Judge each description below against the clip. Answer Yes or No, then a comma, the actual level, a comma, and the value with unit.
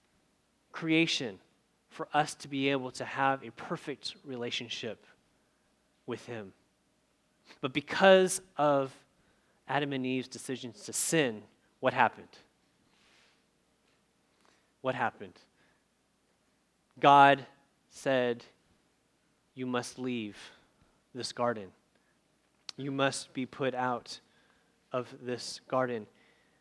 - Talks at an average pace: No, slow, 90 wpm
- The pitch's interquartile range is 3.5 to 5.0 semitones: No, average, 3.1 semitones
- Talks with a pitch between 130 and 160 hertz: Yes, low, 135 Hz